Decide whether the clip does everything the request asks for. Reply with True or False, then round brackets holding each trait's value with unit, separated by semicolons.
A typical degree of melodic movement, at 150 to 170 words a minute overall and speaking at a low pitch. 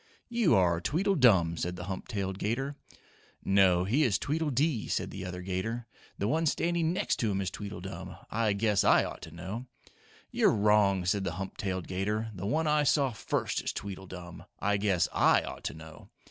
False (5.0 semitones; 185 wpm; 100 Hz)